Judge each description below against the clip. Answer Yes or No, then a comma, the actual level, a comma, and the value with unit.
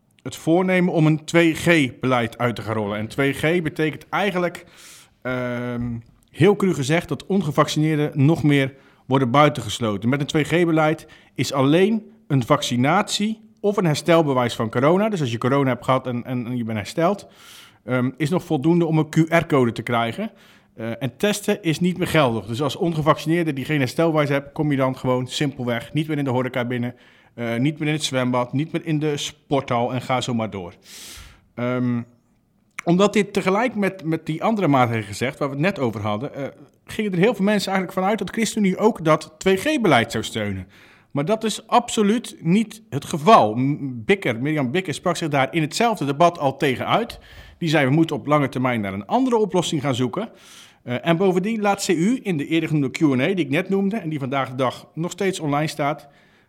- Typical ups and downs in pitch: No, wide, 5.7 semitones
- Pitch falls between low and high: Yes, medium, 150 Hz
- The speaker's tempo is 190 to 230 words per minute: Yes, average, 195 wpm